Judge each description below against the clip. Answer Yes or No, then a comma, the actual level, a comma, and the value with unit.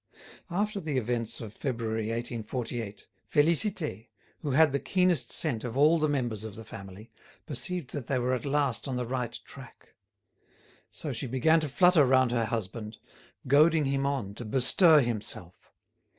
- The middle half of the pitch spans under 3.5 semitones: No, average, 4.8 semitones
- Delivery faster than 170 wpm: No, average, 160 wpm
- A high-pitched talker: No, low, 130 Hz